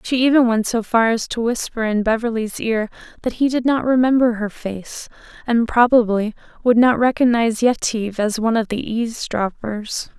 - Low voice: No, high, 230 Hz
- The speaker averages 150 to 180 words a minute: Yes, average, 170 wpm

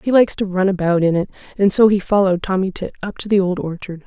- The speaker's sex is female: Yes, female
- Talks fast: Yes, fast, 265 wpm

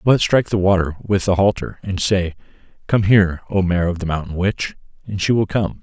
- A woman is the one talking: No, male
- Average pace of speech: No, fast, 215 wpm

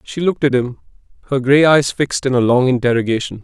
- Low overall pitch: Yes, low, 130 Hz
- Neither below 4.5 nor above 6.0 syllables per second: No, 6.4 syllables/s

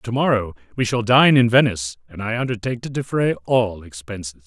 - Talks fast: No, average, 190 wpm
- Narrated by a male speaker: Yes, male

